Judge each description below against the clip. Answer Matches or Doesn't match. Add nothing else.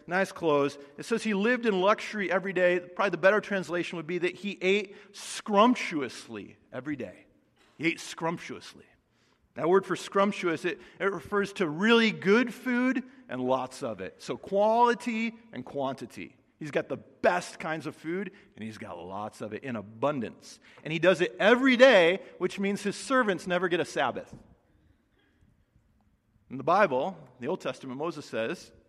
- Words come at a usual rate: Matches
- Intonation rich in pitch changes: Matches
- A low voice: Doesn't match